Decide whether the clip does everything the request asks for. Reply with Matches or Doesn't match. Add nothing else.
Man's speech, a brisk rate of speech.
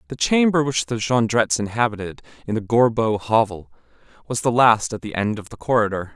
Doesn't match